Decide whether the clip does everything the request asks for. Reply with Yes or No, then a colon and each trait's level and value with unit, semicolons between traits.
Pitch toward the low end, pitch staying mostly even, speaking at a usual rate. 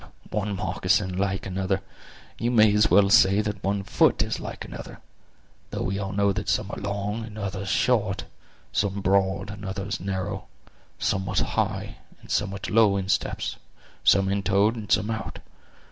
Yes: low, 100 Hz; narrow, 1.3 semitones; average, 165 wpm